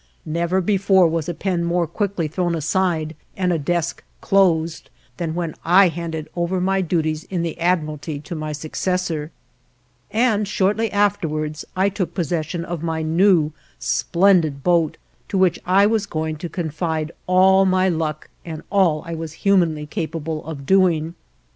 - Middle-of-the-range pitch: Yes, medium, 170 Hz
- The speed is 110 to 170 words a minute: Yes, average, 155 wpm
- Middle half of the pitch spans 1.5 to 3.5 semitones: Yes, average, 2.9 semitones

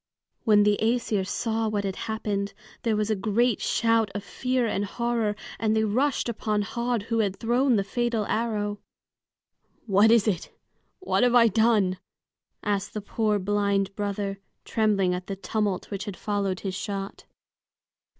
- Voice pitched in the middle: No, high, 210 Hz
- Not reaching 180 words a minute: Yes, average, 160 wpm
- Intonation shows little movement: Yes, narrow, 2.3 semitones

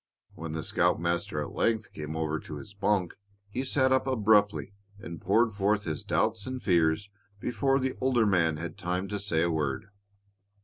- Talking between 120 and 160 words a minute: No, average, 175 wpm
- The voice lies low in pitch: Yes, low, 100 Hz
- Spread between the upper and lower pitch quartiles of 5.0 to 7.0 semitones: Yes, average, 5.3 semitones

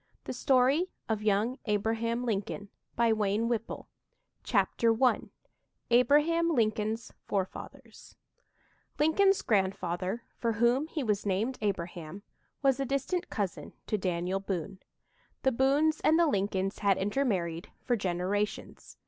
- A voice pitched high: Yes, high, 220 Hz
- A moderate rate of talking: No, slow, 110 wpm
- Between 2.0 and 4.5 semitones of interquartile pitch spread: No, average, 5.3 semitones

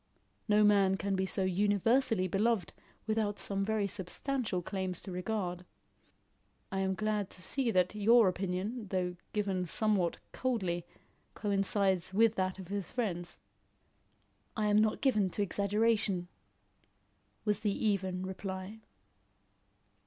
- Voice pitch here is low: No, high, 200 Hz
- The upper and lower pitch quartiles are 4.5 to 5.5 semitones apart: No, narrow, 2.4 semitones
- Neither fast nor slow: No, slow, 125 wpm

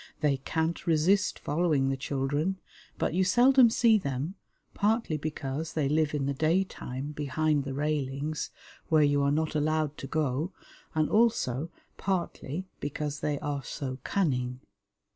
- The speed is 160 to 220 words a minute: No, average, 145 wpm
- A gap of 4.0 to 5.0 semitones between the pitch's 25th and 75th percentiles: No, average, 3.2 semitones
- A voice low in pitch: No, medium, 150 Hz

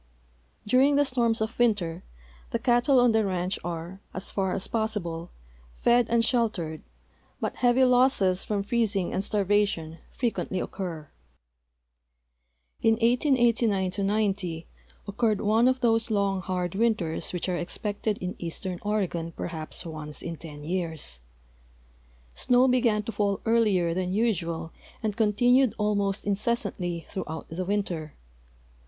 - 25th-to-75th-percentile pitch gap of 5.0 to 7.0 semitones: No, average, 4.6 semitones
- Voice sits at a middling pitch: No, high, 200 Hz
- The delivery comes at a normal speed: No, slow, 130 wpm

